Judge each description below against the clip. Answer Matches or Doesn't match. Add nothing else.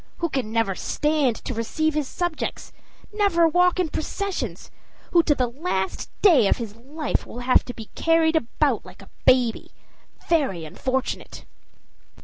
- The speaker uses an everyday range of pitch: Doesn't match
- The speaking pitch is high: Matches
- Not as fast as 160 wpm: Matches